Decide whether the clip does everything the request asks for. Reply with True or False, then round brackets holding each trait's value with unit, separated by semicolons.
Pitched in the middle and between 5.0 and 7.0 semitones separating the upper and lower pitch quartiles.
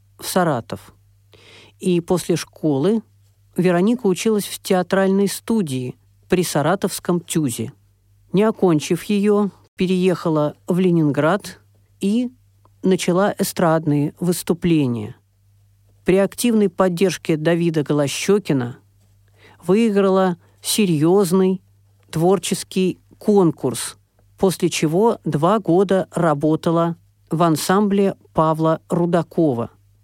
False (170 Hz; 8.2 semitones)